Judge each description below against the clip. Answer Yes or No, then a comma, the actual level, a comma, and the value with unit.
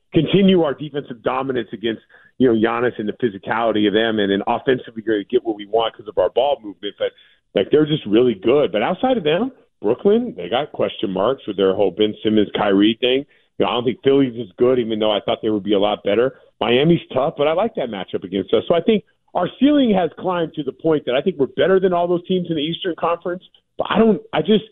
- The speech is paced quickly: Yes, fast, 250 wpm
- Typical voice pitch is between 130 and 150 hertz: Yes, medium, 140 Hz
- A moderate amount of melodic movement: No, wide, 8.5 semitones